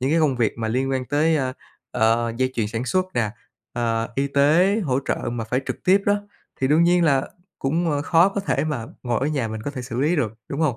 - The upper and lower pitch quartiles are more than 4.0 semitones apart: Yes, average, 5.1 semitones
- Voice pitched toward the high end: No, low, 135 Hz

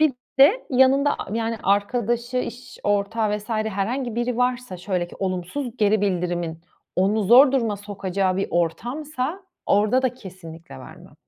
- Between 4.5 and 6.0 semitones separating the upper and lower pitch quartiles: Yes, average, 4.8 semitones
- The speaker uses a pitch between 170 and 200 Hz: No, high, 215 Hz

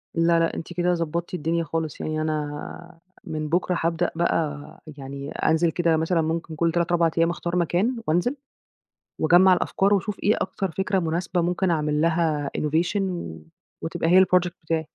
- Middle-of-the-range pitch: Yes, medium, 165 Hz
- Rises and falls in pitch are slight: Yes, narrow, 1.8 semitones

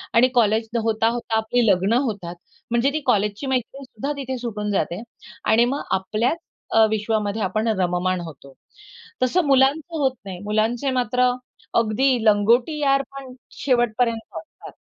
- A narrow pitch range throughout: No, average, 3.6 semitones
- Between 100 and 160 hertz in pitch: No, high, 230 Hz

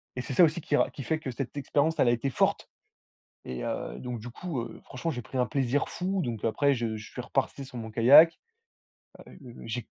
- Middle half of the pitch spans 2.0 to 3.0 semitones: No, average, 3.5 semitones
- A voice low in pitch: Yes, low, 130 Hz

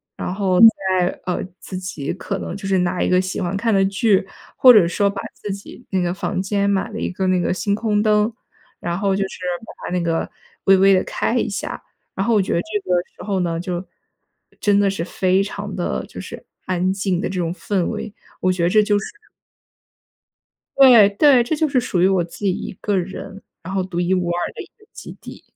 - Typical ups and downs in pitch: No, narrow, 2.2 semitones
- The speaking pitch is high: Yes, high, 195 Hz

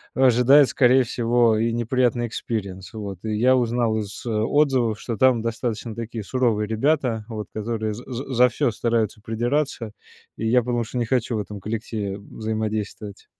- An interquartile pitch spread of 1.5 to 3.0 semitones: Yes, narrow, 2.4 semitones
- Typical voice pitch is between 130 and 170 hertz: No, low, 115 Hz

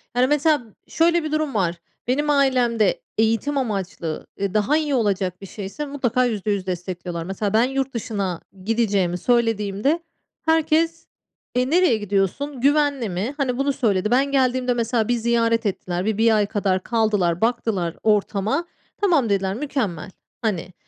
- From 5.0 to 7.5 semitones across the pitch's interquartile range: Yes, wide, 5.6 semitones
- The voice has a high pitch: Yes, high, 230 Hz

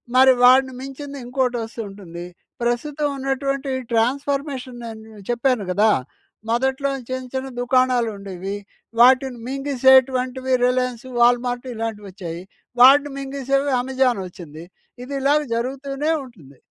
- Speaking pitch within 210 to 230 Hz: No, very high, 255 Hz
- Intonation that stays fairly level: No, average, 3.0 semitones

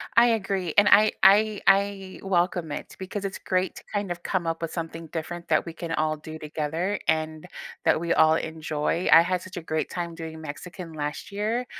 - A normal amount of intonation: Yes, average, 3.3 semitones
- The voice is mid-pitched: Yes, medium, 170 Hz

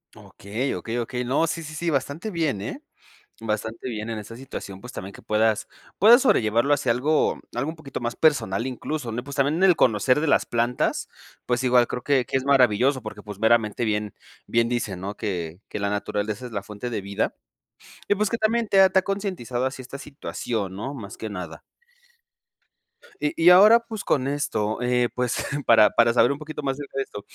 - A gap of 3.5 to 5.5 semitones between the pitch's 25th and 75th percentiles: Yes, average, 5.1 semitones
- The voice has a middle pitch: No, low, 125 Hz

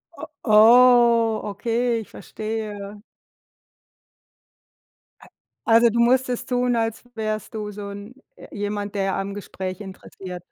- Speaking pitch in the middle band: No, high, 215 Hz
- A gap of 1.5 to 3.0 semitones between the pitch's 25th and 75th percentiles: Yes, narrow, 2.6 semitones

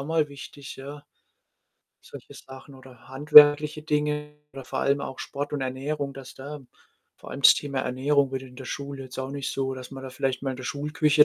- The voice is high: No, medium, 140 Hz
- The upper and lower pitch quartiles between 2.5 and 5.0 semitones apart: No, narrow, 1.8 semitones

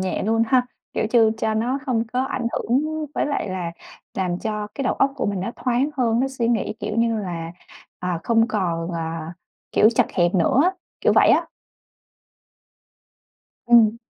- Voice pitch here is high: Yes, high, 220 Hz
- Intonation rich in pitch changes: No, average, 4.6 semitones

